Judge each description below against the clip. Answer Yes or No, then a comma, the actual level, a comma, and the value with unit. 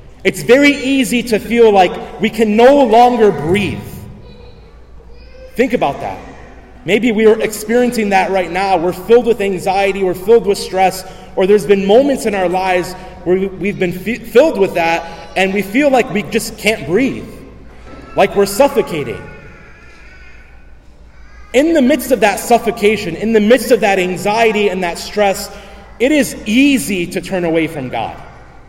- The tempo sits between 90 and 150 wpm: No, average, 160 wpm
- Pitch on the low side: No, high, 205 Hz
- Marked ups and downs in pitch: No, average, 3.9 semitones